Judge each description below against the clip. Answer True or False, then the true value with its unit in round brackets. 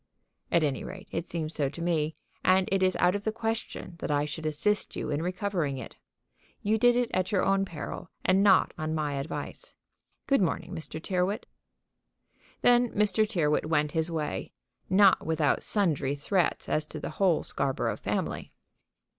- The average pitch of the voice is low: False (170 Hz)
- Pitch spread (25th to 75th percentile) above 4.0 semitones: True (4.4 semitones)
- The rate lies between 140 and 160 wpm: False (170 wpm)